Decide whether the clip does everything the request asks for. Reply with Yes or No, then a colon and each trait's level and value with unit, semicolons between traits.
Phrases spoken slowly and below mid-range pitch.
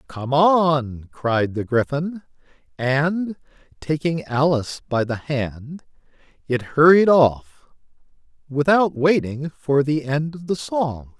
No: slow, 120 wpm; medium, 145 Hz